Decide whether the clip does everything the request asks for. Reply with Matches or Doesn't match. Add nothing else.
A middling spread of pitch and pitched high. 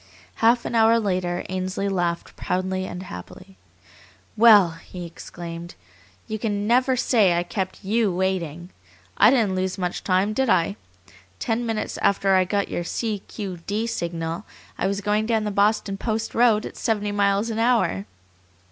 Matches